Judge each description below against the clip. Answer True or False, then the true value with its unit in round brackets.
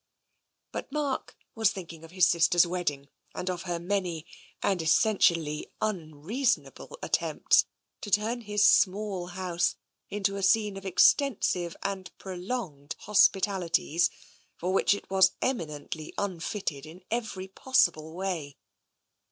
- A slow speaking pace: True (125 wpm)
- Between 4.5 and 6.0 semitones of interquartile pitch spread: False (3.4 semitones)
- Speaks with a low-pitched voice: False (185 Hz)